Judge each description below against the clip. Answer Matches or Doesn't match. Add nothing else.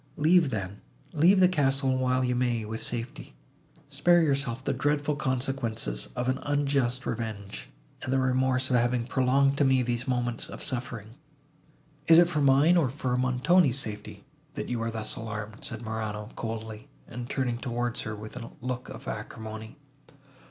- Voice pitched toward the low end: Matches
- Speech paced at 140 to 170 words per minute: Matches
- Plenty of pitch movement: Doesn't match